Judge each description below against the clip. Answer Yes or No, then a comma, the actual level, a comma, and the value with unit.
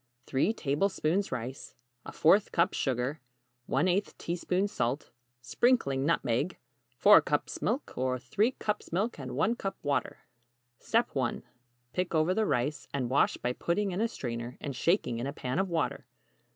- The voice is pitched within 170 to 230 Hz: No, medium, 150 Hz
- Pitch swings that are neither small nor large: No, wide, 7.0 semitones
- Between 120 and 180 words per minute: Yes, average, 150 wpm